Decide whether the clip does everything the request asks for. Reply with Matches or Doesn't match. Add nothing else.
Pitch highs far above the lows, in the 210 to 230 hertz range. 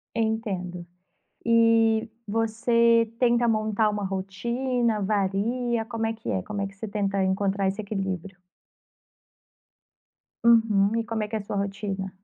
Doesn't match